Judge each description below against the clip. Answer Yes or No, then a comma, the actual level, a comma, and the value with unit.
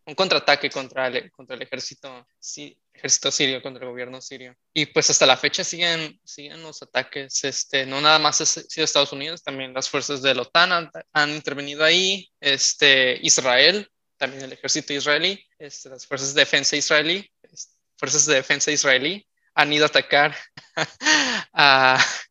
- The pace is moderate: Yes, average, 170 wpm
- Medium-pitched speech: Yes, medium, 145 Hz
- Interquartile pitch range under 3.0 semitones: Yes, narrow, 2.6 semitones